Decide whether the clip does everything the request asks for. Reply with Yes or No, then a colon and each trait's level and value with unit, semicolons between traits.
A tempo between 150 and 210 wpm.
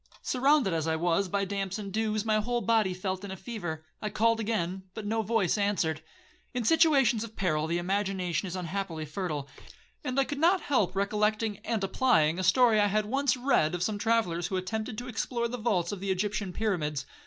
Yes: average, 200 wpm